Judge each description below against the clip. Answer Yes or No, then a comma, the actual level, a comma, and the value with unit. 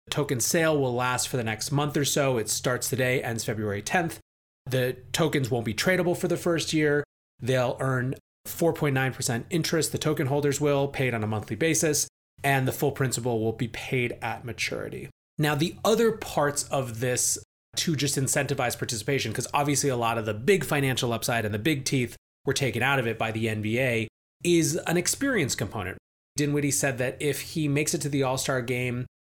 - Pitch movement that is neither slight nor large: Yes, average, 3.6 semitones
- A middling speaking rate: Yes, average, 190 wpm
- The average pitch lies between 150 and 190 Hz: No, low, 135 Hz